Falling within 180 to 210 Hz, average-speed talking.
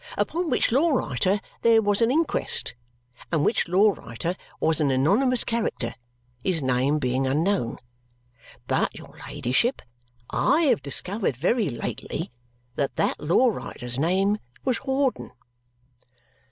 No: medium, 185 Hz; slow, 125 wpm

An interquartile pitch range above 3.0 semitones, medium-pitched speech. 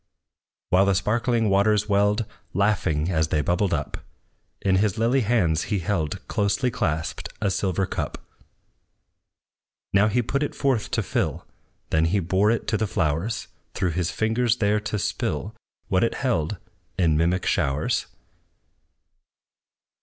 No: average, 3.9 semitones; low, 100 Hz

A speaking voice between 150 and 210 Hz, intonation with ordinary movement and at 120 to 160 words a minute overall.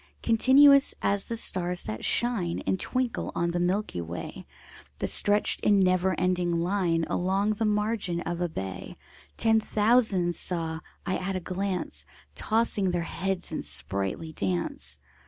Yes: medium, 185 Hz; average, 3.5 semitones; average, 145 wpm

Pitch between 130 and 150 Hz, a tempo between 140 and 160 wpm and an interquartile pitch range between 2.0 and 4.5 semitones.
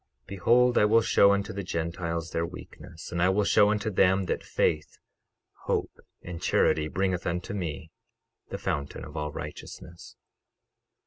No: very low, 90 Hz; average, 150 wpm; average, 3.2 semitones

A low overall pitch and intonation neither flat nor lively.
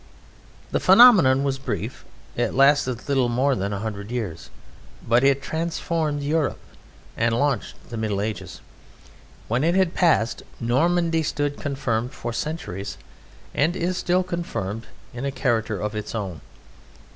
No: low, 130 Hz; wide, 6.0 semitones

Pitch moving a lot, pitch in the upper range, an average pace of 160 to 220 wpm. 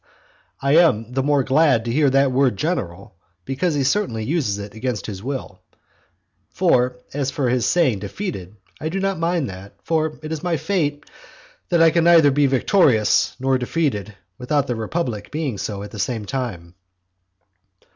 No: wide, 6.2 semitones; low, 135 Hz; average, 170 wpm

